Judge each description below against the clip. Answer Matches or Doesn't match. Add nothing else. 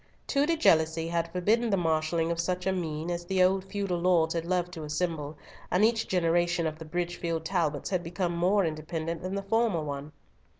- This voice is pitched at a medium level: Matches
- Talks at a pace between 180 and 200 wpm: Matches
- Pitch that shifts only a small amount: Matches